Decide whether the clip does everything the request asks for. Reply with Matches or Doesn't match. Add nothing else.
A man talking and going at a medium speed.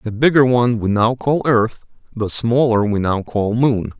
Matches